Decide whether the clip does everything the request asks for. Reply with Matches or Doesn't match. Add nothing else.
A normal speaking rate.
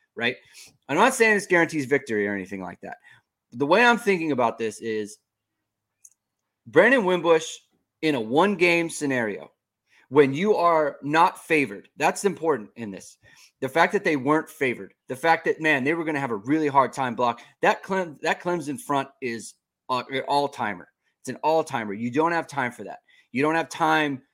Matches